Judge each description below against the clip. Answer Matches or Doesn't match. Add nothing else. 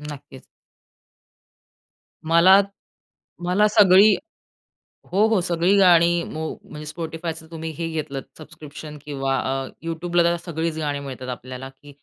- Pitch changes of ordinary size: Matches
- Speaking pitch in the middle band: Matches